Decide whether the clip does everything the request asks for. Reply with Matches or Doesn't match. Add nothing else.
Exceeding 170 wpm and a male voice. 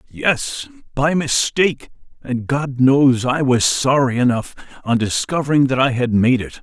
Doesn't match